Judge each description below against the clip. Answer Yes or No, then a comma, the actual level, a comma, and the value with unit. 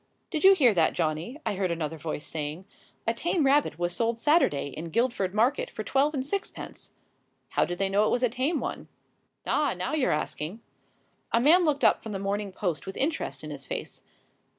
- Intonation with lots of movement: Yes, wide, 8.5 semitones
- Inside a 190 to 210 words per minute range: Yes, average, 200 wpm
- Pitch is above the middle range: Yes, high, 225 Hz